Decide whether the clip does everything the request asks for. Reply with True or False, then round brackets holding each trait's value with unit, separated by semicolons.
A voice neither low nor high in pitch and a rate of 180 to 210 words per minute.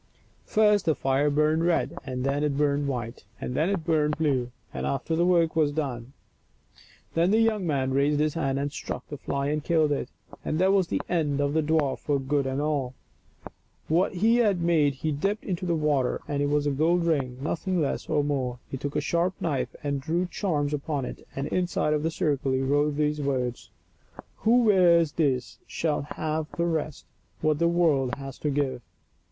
True (150 Hz; 205 wpm)